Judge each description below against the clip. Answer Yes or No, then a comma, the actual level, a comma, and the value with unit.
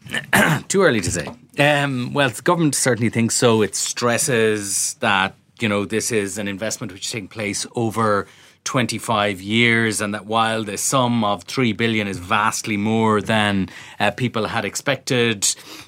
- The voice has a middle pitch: No, low, 110 Hz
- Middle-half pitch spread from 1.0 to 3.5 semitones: Yes, narrow, 2.5 semitones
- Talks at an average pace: Yes, average, 165 wpm